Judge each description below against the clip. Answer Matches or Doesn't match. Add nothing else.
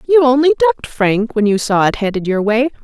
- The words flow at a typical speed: Doesn't match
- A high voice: Matches